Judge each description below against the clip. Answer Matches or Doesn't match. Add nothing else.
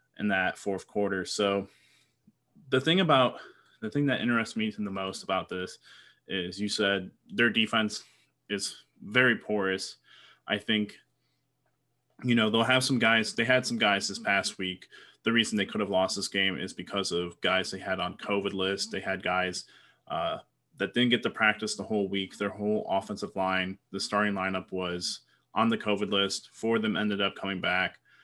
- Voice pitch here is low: Matches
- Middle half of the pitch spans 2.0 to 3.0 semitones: Matches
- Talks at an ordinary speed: Matches